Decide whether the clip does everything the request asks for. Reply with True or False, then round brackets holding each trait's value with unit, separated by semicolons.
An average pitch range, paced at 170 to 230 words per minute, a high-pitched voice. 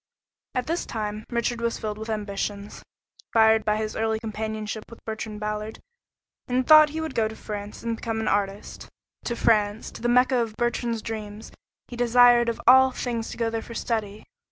False (2.0 semitones; 180 wpm; 225 Hz)